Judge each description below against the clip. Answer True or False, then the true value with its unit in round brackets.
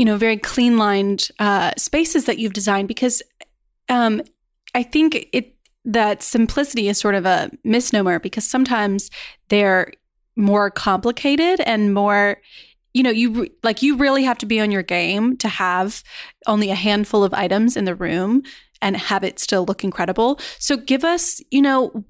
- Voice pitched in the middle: False (220 Hz)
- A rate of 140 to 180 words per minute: True (170 wpm)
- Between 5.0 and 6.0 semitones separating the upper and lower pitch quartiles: False (4.2 semitones)